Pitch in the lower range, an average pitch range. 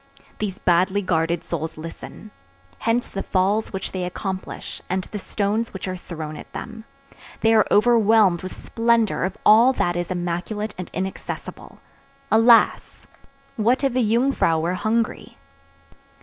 No: high, 200 Hz; average, 3.9 semitones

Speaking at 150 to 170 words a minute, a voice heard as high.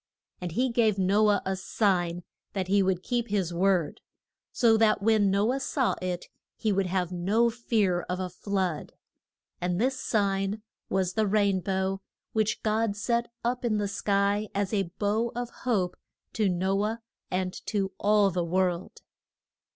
Yes: average, 165 wpm; high, 200 Hz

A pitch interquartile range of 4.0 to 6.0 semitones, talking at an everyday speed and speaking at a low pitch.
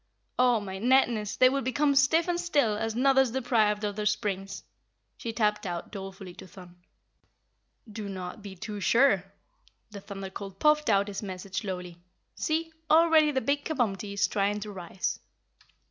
No: average, 5.3 semitones; average, 160 wpm; high, 210 Hz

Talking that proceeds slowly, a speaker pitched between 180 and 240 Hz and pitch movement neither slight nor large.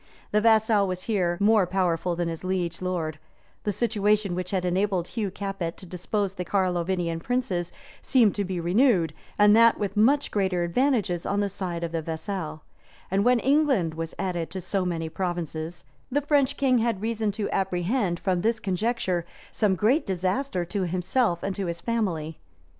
No: average, 175 wpm; high, 190 Hz; average, 3.7 semitones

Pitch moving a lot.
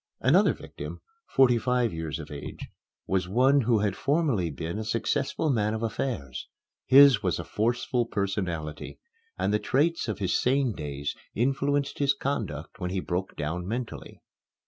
Yes: wide, 6.8 semitones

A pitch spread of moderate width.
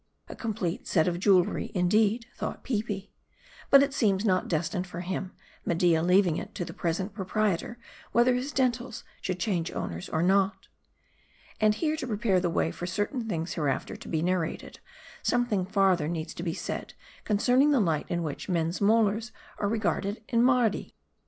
Yes: average, 4.4 semitones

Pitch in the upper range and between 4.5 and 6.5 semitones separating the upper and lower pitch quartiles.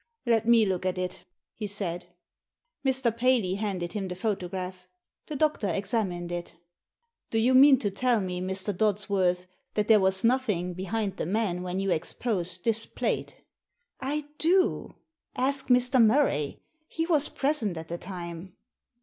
Yes: high, 200 Hz; average, 5.1 semitones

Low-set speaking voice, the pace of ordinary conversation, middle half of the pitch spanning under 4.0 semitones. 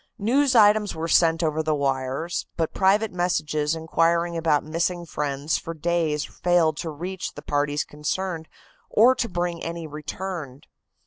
No: medium, 165 Hz; average, 145 wpm; average, 2.9 semitones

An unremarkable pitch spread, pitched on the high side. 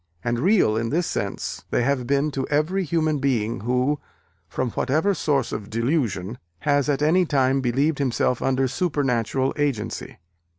No: average, 3.7 semitones; low, 135 Hz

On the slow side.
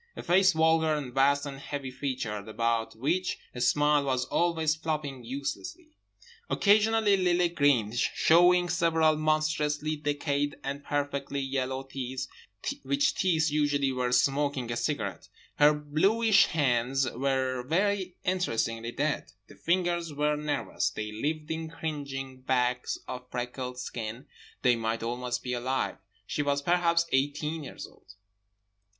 Yes: slow, 130 wpm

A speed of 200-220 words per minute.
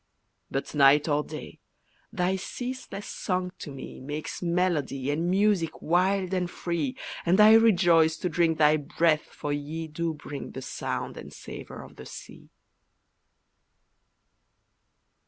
No: slow, 135 wpm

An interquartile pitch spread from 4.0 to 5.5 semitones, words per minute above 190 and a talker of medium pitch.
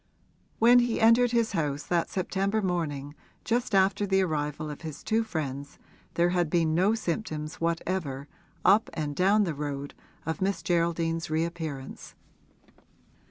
No: average, 4.5 semitones; average, 140 wpm; medium, 170 Hz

